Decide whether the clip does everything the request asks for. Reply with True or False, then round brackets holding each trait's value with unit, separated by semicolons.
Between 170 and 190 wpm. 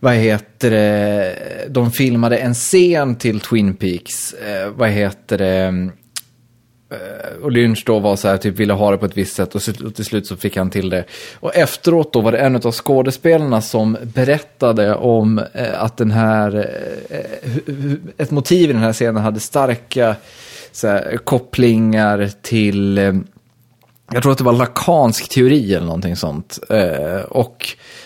False (155 wpm)